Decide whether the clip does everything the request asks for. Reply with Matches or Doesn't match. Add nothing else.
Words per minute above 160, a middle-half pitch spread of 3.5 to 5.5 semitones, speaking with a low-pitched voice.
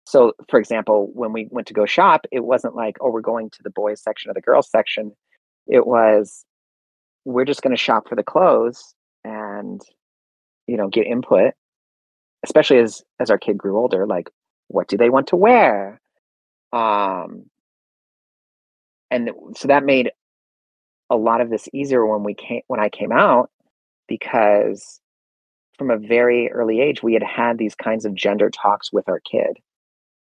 Doesn't match